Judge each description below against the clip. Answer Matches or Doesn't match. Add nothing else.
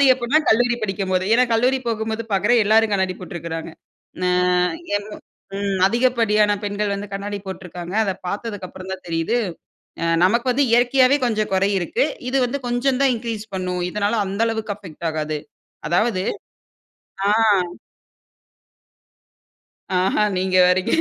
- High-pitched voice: Matches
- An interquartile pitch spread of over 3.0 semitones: Matches